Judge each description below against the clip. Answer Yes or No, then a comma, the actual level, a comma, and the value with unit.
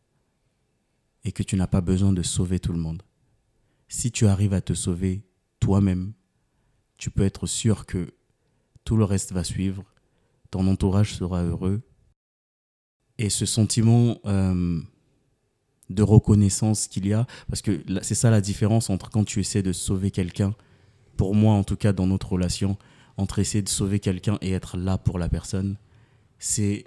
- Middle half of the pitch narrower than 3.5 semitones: Yes, average, 2.8 semitones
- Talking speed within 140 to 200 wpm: Yes, average, 165 wpm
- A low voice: Yes, low, 100 Hz